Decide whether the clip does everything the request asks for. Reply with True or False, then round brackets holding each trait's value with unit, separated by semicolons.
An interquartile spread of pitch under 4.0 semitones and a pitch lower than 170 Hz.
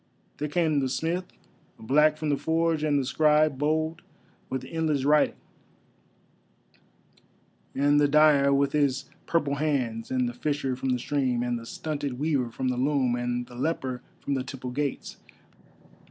True (3.0 semitones; 140 Hz)